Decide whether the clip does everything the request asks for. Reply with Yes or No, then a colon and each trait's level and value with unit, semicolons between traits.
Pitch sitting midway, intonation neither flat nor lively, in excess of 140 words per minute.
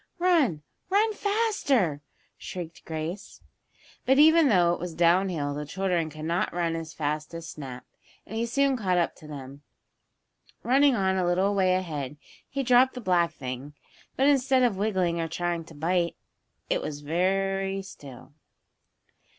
No: medium, 180 Hz; wide, 6.7 semitones; average, 160 wpm